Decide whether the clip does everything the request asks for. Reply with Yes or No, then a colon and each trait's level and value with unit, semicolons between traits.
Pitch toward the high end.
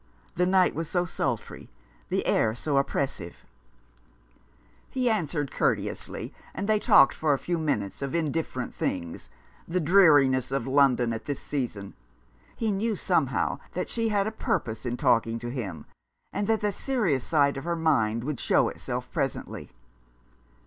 No: medium, 145 Hz